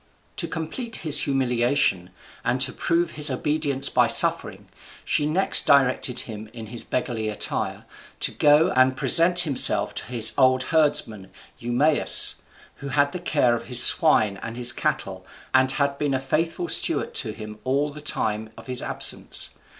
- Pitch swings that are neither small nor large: Yes, average, 4.0 semitones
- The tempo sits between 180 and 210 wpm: No, average, 160 wpm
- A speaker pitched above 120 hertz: Yes, low, 135 Hz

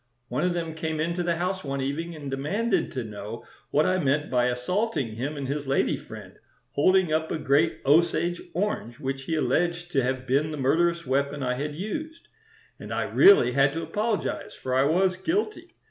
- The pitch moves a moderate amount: Yes, average, 4.5 semitones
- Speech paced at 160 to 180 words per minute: No, average, 190 wpm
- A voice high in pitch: No, medium, 155 Hz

